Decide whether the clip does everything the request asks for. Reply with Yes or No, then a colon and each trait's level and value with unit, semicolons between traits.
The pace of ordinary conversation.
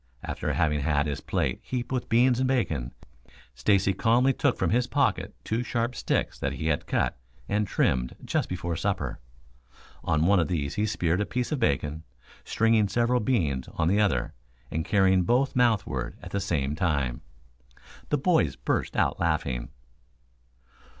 Yes: average, 165 wpm